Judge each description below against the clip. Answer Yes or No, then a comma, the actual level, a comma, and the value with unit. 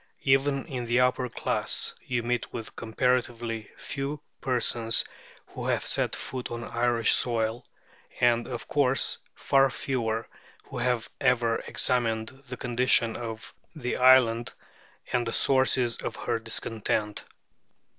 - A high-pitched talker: No, low, 120 Hz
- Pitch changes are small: Yes, narrow, 1.9 semitones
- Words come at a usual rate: No, slow, 125 wpm